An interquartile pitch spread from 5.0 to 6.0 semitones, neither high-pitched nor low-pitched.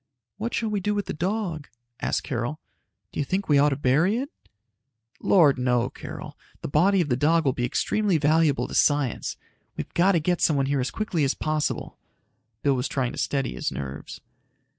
Yes: wide, 5.4 semitones; medium, 150 Hz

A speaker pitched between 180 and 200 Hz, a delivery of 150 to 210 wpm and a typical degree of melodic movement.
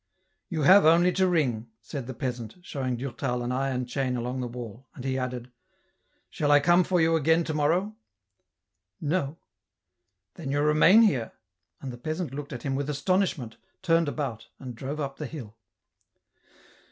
No: medium, 140 Hz; average, 190 wpm; average, 4.5 semitones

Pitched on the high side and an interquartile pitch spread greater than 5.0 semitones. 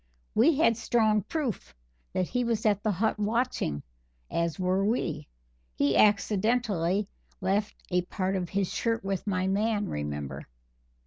No: high, 200 Hz; average, 3.6 semitones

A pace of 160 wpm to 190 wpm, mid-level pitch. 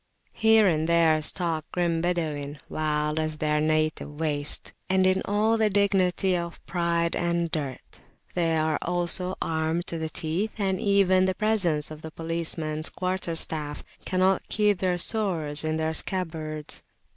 No: average, 145 wpm; medium, 170 Hz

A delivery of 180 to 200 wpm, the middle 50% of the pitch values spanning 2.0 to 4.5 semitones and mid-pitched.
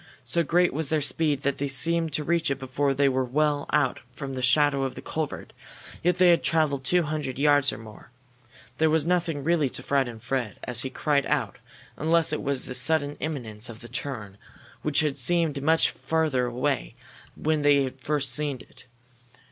Yes: average, 195 wpm; average, 3.2 semitones; medium, 145 Hz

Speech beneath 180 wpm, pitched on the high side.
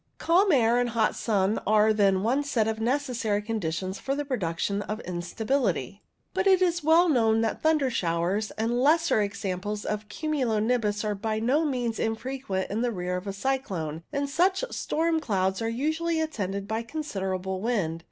Yes: average, 170 wpm; high, 225 Hz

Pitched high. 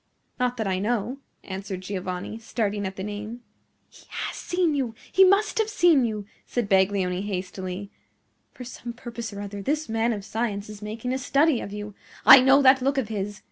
Yes: high, 220 Hz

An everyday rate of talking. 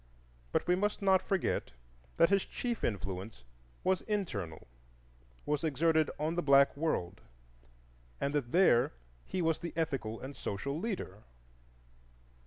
No: slow, 125 wpm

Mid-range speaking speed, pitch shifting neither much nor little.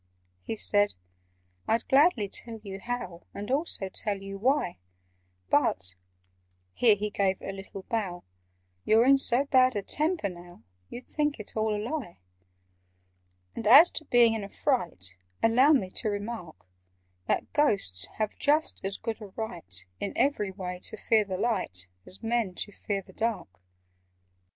Yes: average, 155 wpm; average, 4.1 semitones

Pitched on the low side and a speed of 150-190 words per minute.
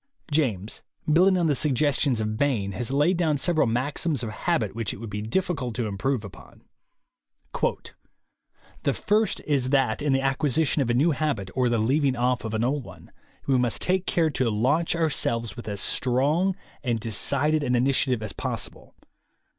Yes: low, 130 Hz; average, 180 wpm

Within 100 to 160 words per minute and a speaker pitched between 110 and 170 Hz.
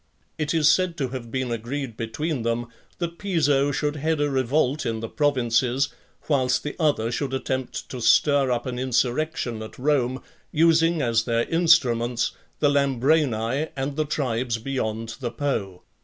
Yes: average, 155 wpm; low, 135 Hz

